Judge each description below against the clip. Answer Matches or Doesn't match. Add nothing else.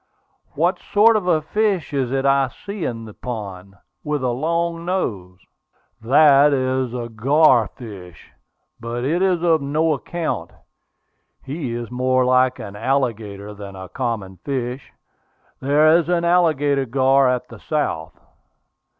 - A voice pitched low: Matches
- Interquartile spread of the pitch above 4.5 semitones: Matches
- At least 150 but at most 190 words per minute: Doesn't match